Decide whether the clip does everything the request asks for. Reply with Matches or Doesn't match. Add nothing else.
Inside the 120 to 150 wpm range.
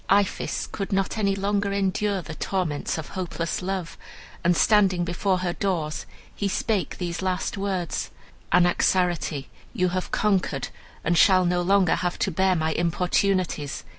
Matches